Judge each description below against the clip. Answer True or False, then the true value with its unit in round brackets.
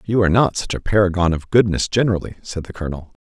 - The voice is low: True (95 Hz)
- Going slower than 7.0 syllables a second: False (7.2 syllables/s)